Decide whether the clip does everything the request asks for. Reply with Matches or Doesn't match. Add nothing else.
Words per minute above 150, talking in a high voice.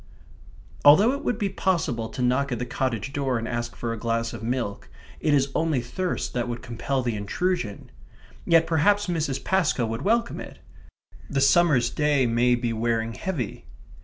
Doesn't match